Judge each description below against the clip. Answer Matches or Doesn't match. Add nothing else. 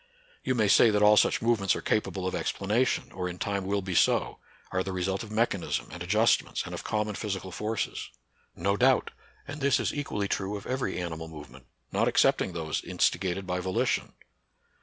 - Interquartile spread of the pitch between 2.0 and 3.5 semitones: Matches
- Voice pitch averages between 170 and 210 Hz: Doesn't match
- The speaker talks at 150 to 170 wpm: Doesn't match